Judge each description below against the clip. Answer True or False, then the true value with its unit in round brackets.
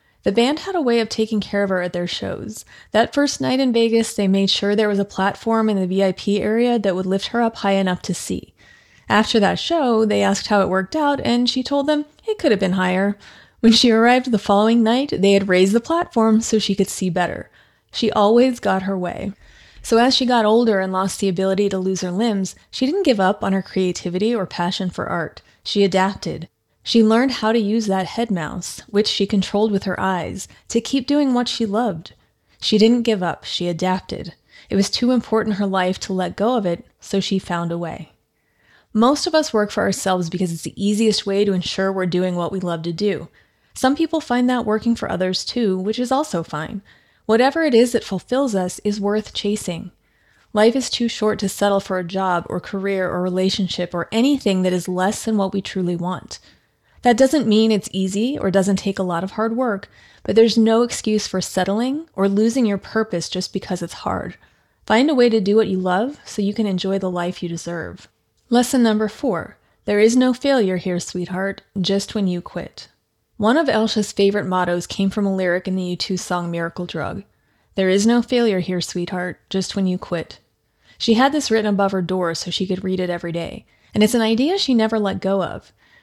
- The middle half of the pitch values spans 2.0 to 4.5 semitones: True (3.6 semitones)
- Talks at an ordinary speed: False (220 wpm)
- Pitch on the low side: False (200 Hz)